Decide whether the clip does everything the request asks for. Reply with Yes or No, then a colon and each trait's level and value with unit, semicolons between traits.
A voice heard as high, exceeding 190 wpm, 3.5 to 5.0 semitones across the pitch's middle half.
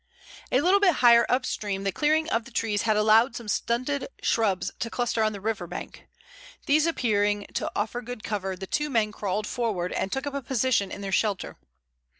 Yes: high, 225 Hz; average, 200 wpm; average, 3.8 semitones